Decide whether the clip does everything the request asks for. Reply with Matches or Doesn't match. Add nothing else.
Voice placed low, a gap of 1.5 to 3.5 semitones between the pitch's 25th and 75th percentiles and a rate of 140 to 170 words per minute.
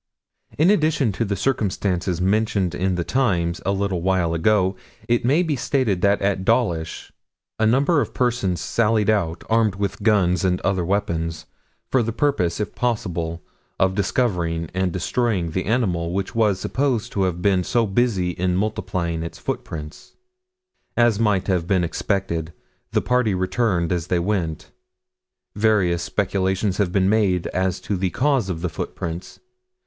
Doesn't match